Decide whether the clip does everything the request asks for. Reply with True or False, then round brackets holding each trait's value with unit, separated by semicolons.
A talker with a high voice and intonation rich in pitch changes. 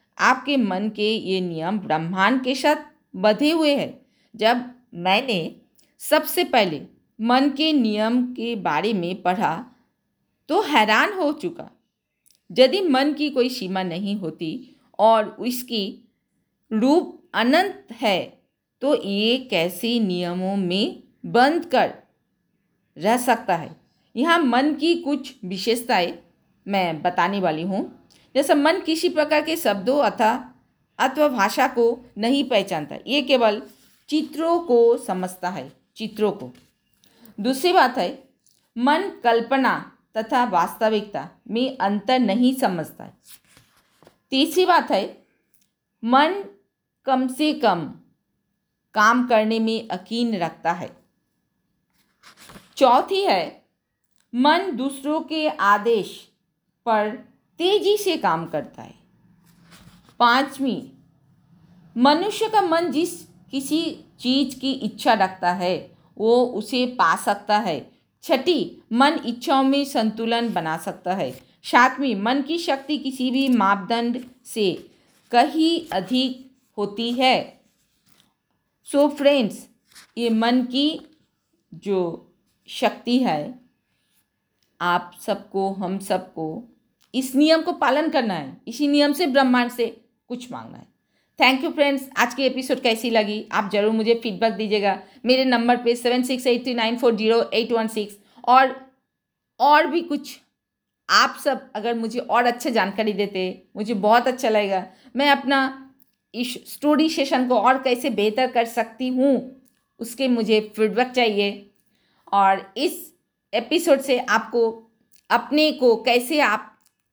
False (240 Hz; 4.7 semitones)